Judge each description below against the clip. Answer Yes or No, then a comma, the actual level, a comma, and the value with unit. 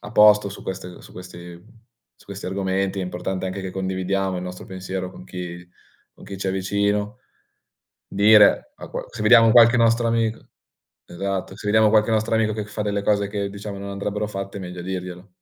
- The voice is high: No, low, 100 Hz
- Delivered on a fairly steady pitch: Yes, narrow, 2.2 semitones